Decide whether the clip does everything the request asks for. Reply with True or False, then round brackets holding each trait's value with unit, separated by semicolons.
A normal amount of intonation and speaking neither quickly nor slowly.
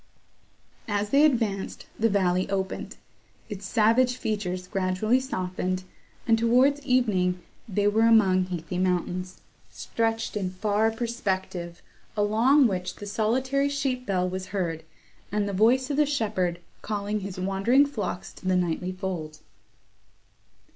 False (3.9 semitones; 130 wpm)